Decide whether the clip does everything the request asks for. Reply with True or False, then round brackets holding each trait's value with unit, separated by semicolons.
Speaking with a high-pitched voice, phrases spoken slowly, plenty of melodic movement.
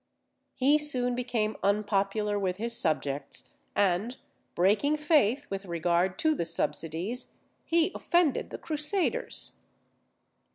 True (215 Hz; 110 wpm; 7.6 semitones)